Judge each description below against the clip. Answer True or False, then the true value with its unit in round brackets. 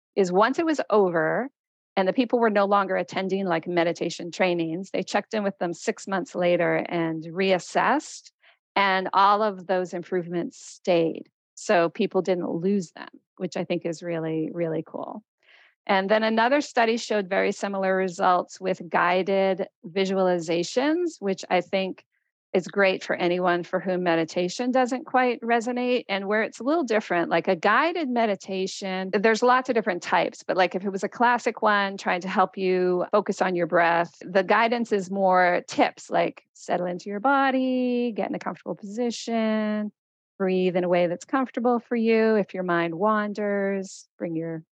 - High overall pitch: True (195 Hz)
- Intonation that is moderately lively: True (3.9 semitones)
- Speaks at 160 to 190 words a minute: True (170 wpm)